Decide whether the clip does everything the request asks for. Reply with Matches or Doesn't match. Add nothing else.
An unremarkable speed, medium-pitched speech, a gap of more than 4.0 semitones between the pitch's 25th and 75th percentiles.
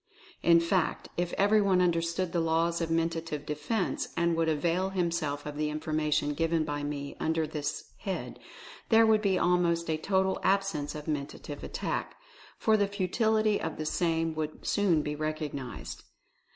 Doesn't match